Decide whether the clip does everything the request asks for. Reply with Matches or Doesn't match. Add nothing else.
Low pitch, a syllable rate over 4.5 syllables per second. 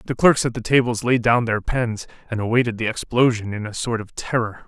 Matches